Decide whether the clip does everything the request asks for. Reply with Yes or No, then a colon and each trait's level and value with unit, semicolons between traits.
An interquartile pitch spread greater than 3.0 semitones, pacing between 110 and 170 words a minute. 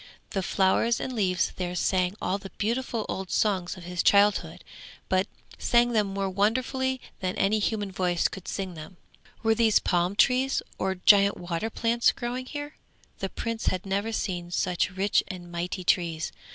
Yes: average, 3.6 semitones; average, 165 wpm